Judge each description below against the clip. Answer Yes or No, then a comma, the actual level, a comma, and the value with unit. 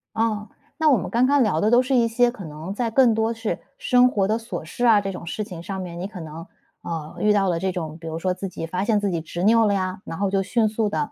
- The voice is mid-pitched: No, high, 205 Hz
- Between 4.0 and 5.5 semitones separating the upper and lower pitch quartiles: Yes, average, 4.3 semitones